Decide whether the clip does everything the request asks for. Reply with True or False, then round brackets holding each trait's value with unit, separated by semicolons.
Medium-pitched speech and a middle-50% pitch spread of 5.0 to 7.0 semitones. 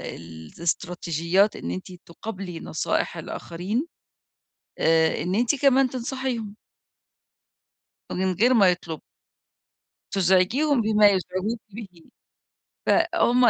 False (195 Hz; 5.6 semitones)